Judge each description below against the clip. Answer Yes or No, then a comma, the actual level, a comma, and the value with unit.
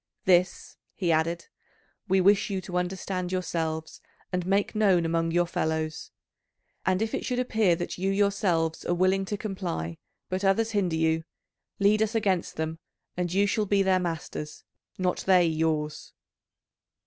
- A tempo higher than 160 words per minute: No, average, 155 wpm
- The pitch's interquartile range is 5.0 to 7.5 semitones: No, average, 3.2 semitones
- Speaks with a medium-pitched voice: Yes, medium, 180 Hz